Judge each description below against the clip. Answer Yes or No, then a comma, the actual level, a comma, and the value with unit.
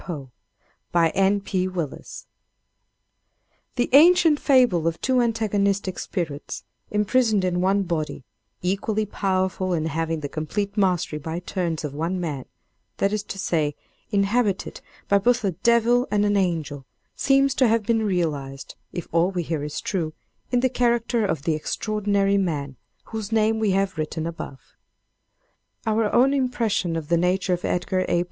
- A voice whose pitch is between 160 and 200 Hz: Yes, high, 190 Hz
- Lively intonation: No, average, 4.9 semitones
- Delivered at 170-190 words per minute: No, average, 155 wpm